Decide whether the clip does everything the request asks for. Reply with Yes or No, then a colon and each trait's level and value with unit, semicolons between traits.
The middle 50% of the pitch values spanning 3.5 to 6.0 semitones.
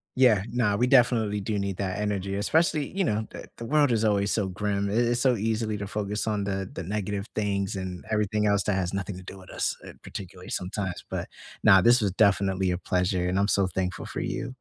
No: narrow, 2.4 semitones